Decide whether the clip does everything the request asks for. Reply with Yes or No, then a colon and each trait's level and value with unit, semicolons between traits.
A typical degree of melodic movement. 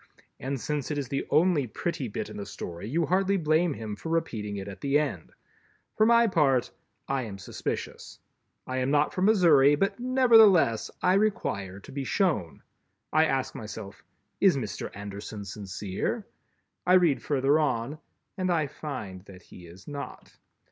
No: wide, 8.4 semitones